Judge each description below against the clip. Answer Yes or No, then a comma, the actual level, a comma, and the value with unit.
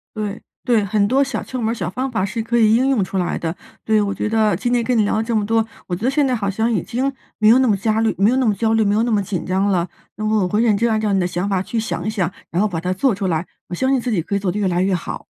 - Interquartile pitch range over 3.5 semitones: No, average, 3.1 semitones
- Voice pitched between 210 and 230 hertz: Yes, high, 215 Hz